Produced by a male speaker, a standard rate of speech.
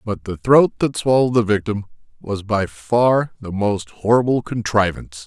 Yes: male; average, 160 wpm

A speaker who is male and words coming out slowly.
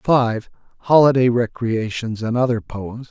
Yes: male; slow, 115 wpm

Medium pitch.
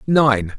No: low, 125 Hz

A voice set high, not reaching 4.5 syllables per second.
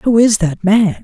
Yes: high, 205 Hz; 4.0 syllables/s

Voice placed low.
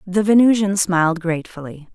No: medium, 185 Hz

